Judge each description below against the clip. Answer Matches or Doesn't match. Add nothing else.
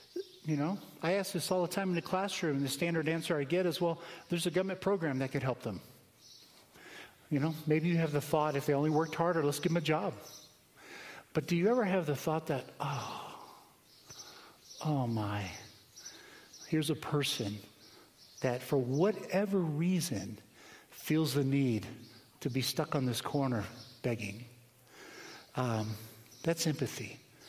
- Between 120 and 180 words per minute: Matches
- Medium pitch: Matches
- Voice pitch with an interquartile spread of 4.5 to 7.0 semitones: Matches